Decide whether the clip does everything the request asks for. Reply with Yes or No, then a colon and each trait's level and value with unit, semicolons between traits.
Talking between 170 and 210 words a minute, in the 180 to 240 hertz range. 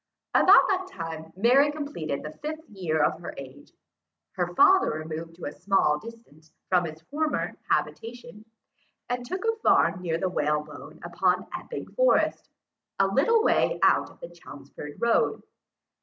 No: average, 155 wpm; high, 190 Hz